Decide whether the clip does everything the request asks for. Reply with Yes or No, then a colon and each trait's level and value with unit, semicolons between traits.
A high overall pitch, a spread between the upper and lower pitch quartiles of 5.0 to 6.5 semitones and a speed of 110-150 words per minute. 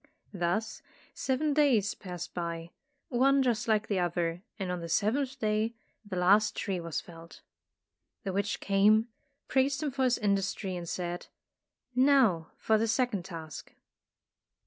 Yes: high, 205 Hz; wide, 5.6 semitones; average, 145 wpm